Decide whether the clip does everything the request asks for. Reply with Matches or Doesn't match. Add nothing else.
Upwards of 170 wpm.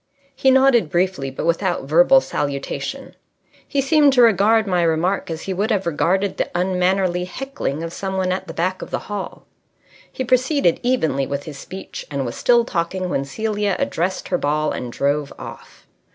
Matches